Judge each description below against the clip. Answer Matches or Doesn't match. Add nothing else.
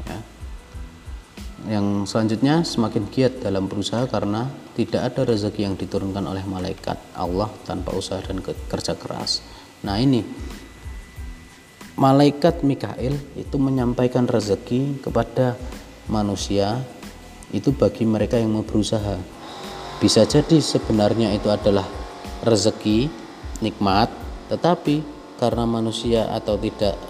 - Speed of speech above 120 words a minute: Doesn't match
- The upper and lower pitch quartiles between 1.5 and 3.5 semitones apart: Doesn't match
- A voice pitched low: Matches